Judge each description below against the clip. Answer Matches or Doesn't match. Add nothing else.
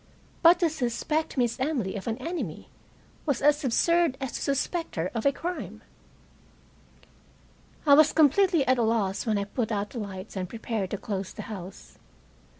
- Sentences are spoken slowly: Doesn't match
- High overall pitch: Matches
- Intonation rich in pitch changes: Matches